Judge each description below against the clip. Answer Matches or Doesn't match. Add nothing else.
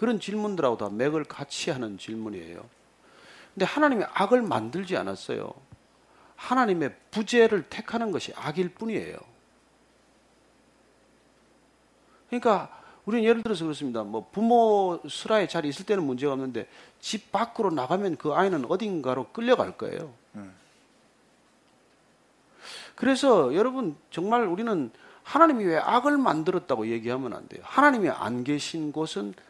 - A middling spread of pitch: Doesn't match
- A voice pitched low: Doesn't match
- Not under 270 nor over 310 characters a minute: Matches